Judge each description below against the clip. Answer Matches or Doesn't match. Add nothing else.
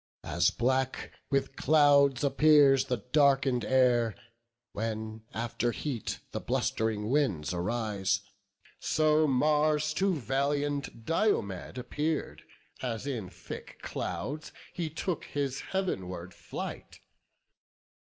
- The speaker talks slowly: Matches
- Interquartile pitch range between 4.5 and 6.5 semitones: Matches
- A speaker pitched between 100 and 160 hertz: Matches